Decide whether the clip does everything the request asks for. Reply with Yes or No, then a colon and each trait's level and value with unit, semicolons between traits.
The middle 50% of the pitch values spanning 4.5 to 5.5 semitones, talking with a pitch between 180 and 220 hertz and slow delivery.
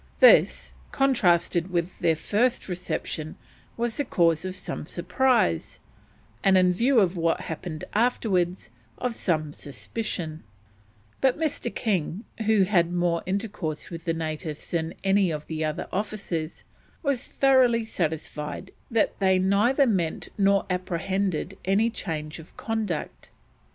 Yes: average, 5.0 semitones; medium, 185 Hz; slow, 130 wpm